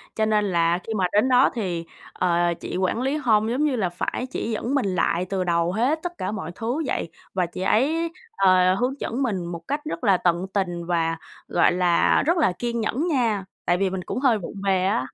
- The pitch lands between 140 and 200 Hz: Yes, high, 195 Hz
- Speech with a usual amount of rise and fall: No, wide, 5.8 semitones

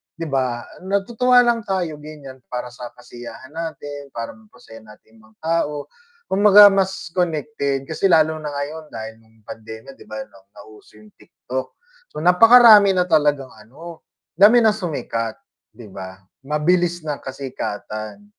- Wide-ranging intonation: Yes, wide, 7.3 semitones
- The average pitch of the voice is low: No, medium, 150 Hz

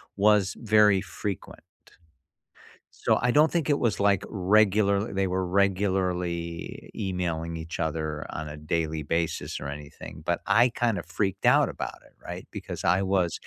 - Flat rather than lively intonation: No, average, 3.7 semitones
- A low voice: Yes, very low, 95 Hz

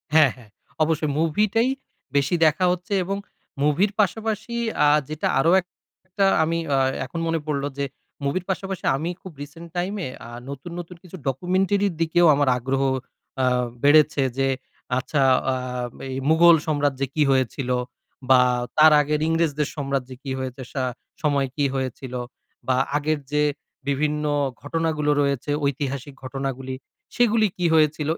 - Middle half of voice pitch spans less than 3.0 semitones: No, average, 3.8 semitones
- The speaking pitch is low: No, medium, 150 Hz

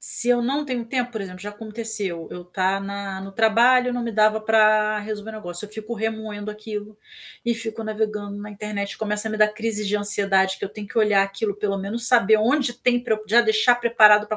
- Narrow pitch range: Yes, narrow, 1.8 semitones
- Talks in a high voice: Yes, high, 215 Hz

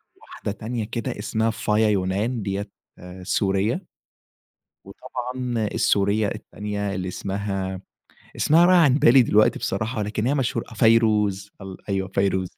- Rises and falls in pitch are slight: No, average, 3.1 semitones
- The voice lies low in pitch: Yes, low, 105 Hz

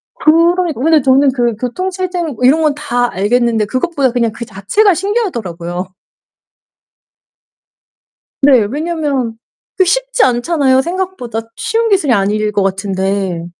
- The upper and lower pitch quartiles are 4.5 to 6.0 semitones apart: No, wide, 7.7 semitones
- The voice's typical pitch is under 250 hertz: No, very high, 260 Hz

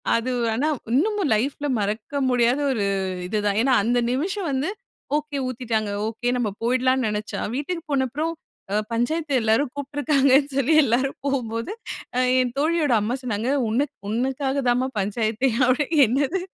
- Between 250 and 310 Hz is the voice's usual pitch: Yes, very high, 260 Hz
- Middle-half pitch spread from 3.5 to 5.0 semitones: Yes, average, 3.8 semitones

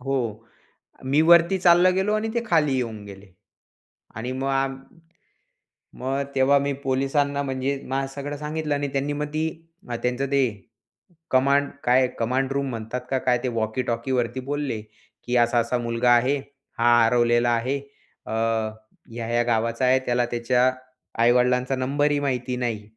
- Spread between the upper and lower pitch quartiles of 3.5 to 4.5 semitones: No, average, 2.9 semitones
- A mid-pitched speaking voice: No, low, 130 Hz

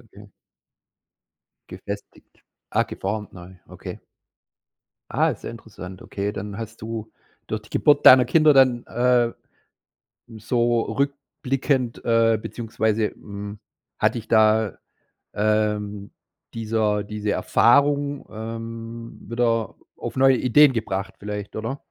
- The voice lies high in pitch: No, low, 115 Hz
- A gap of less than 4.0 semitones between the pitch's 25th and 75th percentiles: Yes, narrow, 2.5 semitones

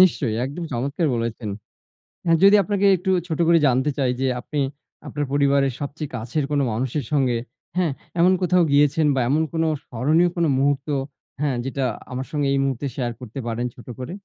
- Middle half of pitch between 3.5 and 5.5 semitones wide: Yes, average, 3.9 semitones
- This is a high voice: No, medium, 140 Hz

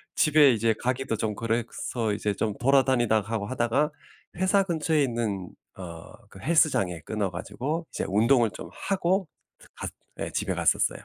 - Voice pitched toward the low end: Yes, low, 120 Hz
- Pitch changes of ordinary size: No, wide, 6.1 semitones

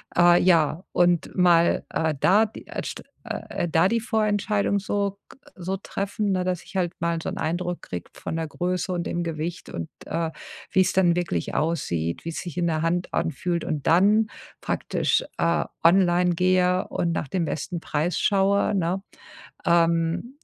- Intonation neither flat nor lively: No, narrow, 2.2 semitones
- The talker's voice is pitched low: No, medium, 175 Hz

